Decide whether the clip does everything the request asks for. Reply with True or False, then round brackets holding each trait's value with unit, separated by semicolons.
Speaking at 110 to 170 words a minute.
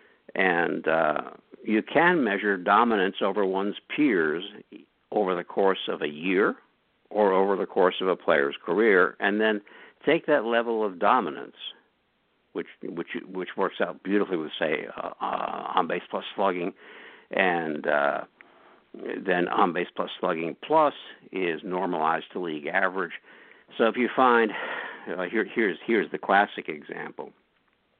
True (145 wpm)